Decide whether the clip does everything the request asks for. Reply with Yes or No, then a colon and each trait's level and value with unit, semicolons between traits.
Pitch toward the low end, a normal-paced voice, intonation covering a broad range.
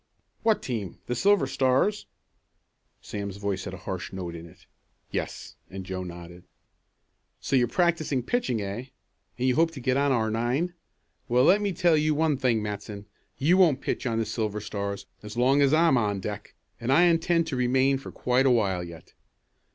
Yes: low, 125 Hz; average, 185 wpm; wide, 6.5 semitones